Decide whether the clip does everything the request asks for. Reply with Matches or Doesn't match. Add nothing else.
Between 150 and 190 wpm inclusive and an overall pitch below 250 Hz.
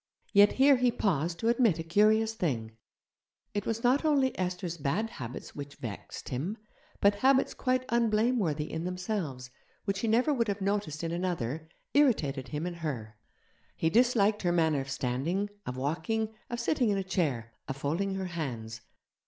Matches